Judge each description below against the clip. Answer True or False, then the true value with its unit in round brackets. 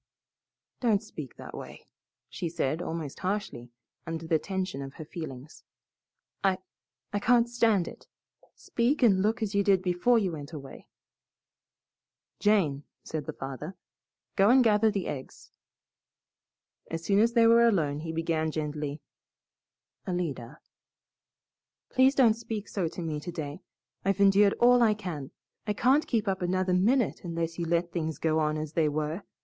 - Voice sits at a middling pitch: True (180 Hz)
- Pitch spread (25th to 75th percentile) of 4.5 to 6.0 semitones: True (5.2 semitones)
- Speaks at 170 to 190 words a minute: False (155 wpm)